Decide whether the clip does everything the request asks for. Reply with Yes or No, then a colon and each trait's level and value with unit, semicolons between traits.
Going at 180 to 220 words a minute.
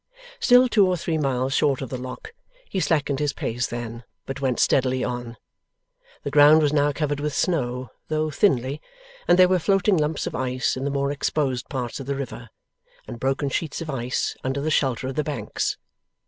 Yes: average, 195 wpm